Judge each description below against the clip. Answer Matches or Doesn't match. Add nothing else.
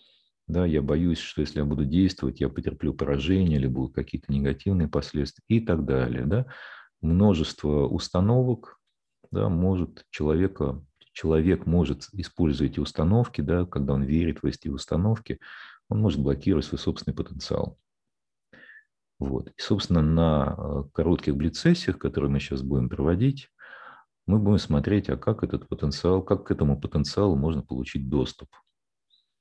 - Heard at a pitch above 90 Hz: Doesn't match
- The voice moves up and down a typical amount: Matches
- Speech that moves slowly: Doesn't match